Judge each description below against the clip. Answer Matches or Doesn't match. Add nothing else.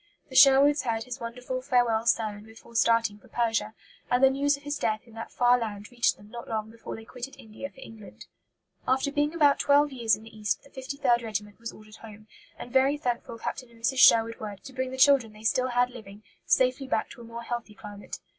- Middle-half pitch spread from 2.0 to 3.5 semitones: Matches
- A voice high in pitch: Matches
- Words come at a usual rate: Doesn't match